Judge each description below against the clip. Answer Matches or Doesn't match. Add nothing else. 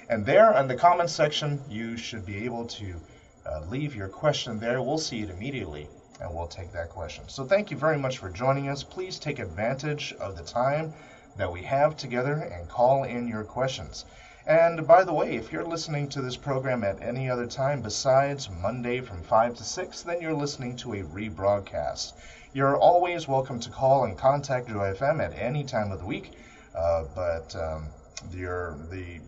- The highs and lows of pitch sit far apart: Matches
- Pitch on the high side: Doesn't match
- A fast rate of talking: Doesn't match